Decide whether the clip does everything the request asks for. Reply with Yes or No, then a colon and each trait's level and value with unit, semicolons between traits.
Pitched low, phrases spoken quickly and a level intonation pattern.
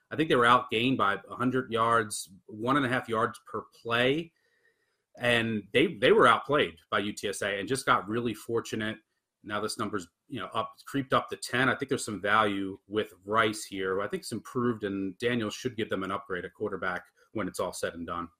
No: low, 115 Hz; fast, 210 wpm; average, 3.3 semitones